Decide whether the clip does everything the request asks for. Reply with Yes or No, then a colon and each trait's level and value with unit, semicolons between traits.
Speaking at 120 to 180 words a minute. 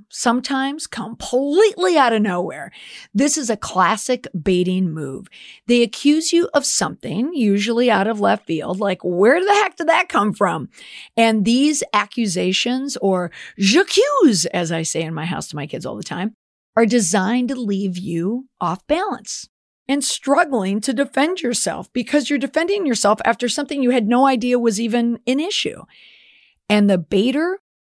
Yes: average, 160 wpm